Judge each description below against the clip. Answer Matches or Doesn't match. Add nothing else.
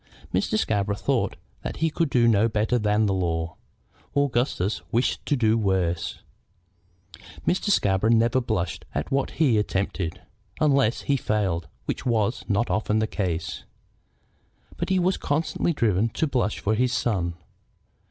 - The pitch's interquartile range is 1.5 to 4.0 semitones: Doesn't match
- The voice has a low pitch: Matches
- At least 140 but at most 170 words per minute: Matches